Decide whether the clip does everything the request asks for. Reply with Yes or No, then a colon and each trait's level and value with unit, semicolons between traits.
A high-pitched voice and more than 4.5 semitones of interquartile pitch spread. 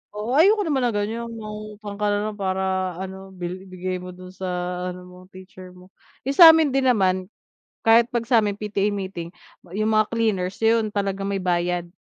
No: high, 200 Hz; average, 3.2 semitones